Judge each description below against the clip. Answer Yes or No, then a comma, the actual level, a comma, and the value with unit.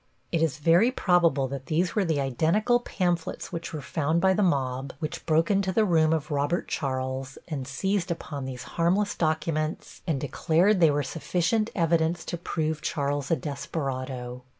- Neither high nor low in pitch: Yes, medium, 160 Hz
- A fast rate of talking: No, average, 170 wpm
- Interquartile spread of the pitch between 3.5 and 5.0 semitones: Yes, average, 3.9 semitones